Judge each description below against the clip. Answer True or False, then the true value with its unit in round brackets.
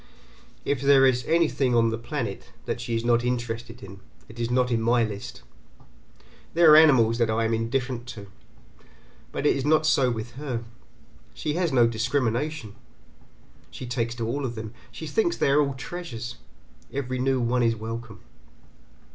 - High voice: False (120 Hz)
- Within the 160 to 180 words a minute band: True (170 wpm)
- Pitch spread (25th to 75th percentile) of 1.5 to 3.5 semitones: True (3.2 semitones)